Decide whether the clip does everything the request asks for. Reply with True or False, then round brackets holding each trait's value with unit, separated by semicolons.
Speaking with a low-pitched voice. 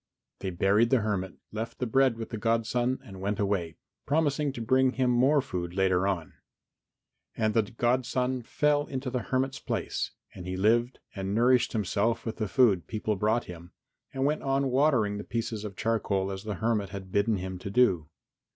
True (115 Hz)